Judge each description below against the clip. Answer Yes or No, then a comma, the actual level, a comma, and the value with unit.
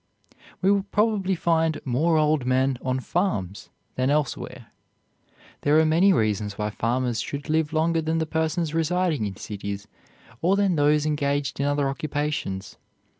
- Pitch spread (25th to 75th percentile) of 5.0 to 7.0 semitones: No, average, 4.2 semitones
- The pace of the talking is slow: No, average, 145 wpm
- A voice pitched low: No, medium, 150 Hz